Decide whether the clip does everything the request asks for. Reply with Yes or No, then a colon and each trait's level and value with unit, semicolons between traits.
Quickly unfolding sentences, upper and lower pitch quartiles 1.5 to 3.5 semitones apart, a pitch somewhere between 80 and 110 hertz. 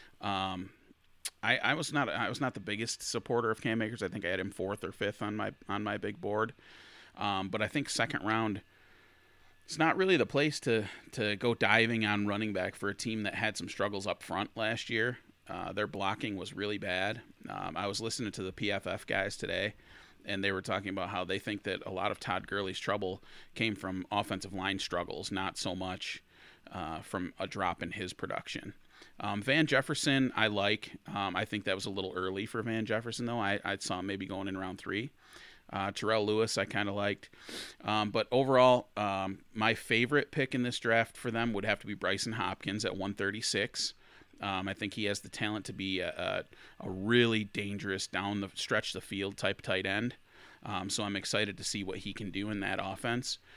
Yes: fast, 210 wpm; average, 2.7 semitones; low, 105 Hz